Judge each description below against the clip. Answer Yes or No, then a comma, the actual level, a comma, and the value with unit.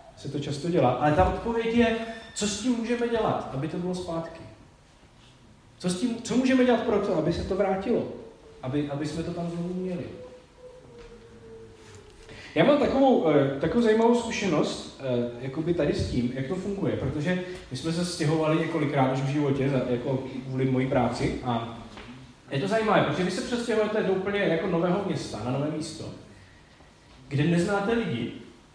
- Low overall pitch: No, medium, 165 Hz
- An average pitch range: No, wide, 7.5 semitones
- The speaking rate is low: No, fast, 170 wpm